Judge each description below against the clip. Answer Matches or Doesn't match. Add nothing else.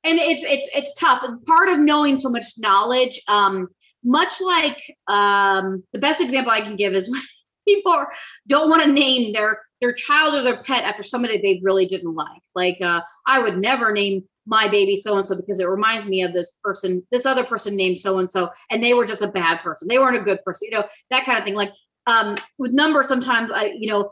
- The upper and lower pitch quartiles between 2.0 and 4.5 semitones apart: Doesn't match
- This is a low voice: Doesn't match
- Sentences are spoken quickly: Matches